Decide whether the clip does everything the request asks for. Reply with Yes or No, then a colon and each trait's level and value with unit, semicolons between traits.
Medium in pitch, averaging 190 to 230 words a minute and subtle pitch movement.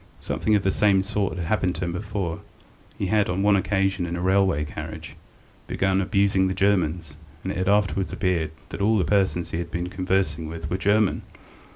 No: very low, 95 Hz; average, 200 wpm; narrow, 2.3 semitones